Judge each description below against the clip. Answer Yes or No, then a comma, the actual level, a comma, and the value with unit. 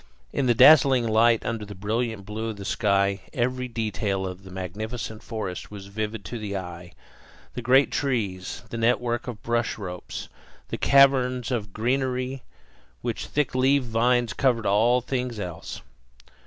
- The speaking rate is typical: Yes, average, 155 wpm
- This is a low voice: Yes, low, 115 Hz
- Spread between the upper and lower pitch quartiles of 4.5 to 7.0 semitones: No, average, 3.8 semitones